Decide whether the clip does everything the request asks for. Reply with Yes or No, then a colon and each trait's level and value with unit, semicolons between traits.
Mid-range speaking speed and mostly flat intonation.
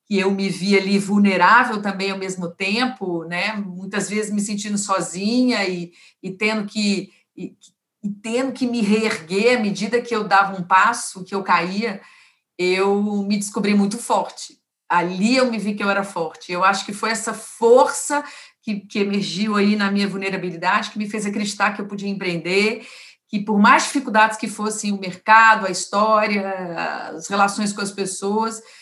Yes: average, 175 wpm; narrow, 2.0 semitones